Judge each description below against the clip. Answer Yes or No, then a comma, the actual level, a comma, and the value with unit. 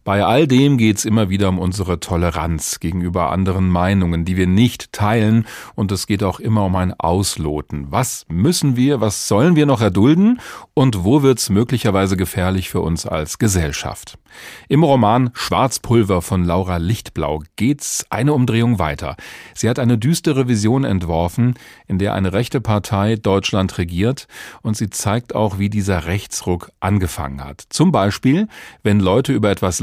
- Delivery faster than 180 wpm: No, average, 160 wpm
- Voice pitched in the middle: No, low, 100 Hz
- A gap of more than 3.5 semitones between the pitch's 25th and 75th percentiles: Yes, average, 4.7 semitones